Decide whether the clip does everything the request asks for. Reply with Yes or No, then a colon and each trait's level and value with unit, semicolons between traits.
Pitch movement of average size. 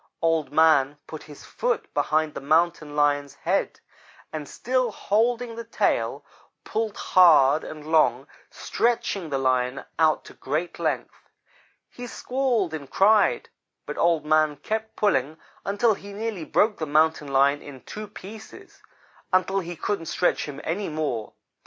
No: wide, 6.2 semitones